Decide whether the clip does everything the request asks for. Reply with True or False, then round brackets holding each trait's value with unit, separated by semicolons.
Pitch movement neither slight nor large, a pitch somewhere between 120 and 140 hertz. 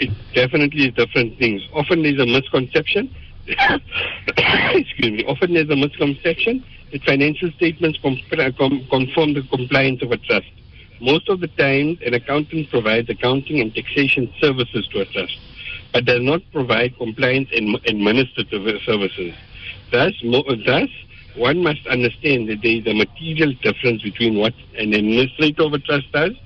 True (4.2 semitones; 135 Hz)